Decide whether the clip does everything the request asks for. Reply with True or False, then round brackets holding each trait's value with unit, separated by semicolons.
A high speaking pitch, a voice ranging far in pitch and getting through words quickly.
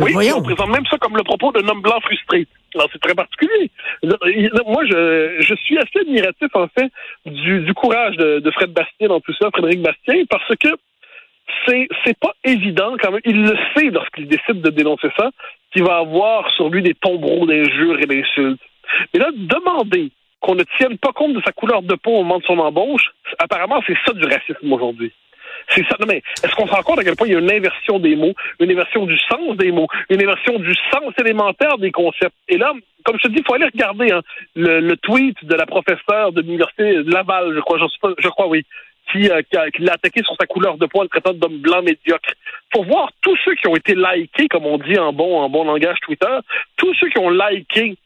True (195 Hz; 6.7 semitones; 230 wpm)